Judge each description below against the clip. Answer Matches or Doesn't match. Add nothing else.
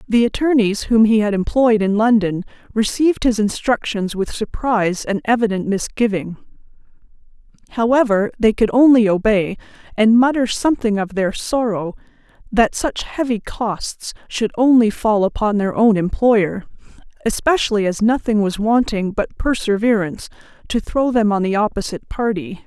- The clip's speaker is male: Doesn't match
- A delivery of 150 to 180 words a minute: Doesn't match